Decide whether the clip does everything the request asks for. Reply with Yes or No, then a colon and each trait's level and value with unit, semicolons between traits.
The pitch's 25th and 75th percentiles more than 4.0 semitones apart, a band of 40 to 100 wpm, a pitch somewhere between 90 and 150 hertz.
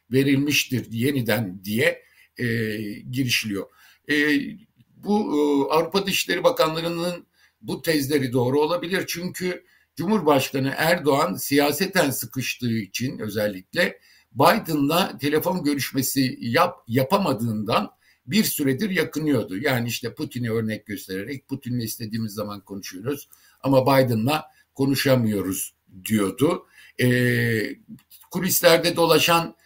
Yes: wide, 5.6 semitones; slow, 95 wpm; low, 135 Hz